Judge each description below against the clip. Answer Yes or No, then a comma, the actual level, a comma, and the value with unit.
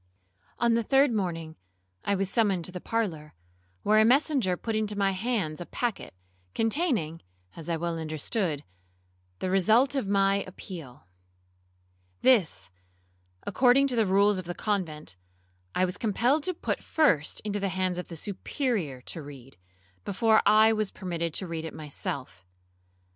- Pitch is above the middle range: Yes, high, 195 Hz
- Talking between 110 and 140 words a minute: No, average, 155 wpm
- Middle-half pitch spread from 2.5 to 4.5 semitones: No, average, 5.2 semitones